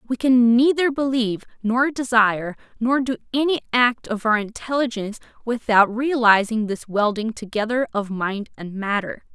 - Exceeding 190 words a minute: No, average, 140 wpm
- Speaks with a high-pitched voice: Yes, high, 230 Hz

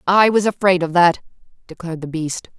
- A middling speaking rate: Yes, average, 185 wpm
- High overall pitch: No, medium, 175 Hz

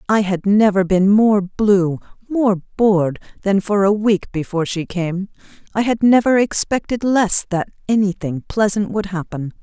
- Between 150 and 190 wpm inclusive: Yes, average, 155 wpm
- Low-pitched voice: No, high, 200 Hz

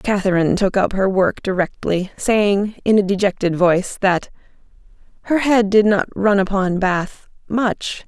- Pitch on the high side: Yes, high, 200 Hz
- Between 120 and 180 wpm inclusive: Yes, average, 140 wpm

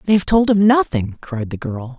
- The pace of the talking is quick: Yes, fast, 240 wpm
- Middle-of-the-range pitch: Yes, medium, 155 Hz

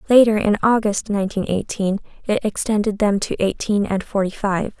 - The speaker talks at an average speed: Yes, average, 165 wpm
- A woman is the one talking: Yes, female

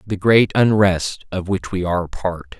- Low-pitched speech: Yes, very low, 95 Hz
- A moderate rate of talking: Yes, average, 185 wpm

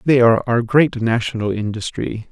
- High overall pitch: No, low, 115 Hz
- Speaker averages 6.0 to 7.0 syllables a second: No, 5.0 syllables/s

